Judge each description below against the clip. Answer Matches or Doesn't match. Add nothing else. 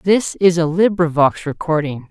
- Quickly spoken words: Doesn't match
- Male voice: Matches